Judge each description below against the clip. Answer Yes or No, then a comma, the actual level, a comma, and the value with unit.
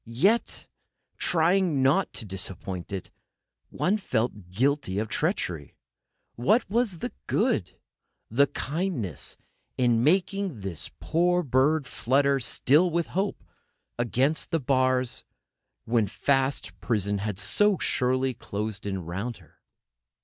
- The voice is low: Yes, low, 130 Hz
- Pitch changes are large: Yes, wide, 7.8 semitones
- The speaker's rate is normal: No, slow, 115 wpm